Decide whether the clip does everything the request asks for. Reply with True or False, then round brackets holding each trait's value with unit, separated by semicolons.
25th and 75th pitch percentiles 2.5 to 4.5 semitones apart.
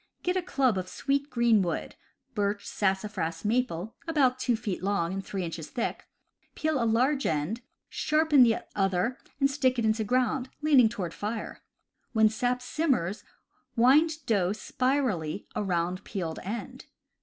False (5.3 semitones)